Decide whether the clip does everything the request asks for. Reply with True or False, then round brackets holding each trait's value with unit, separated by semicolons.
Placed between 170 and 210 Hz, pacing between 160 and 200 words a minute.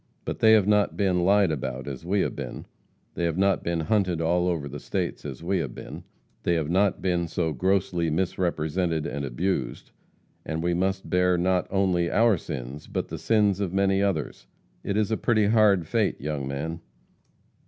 False (90 Hz; 185 wpm)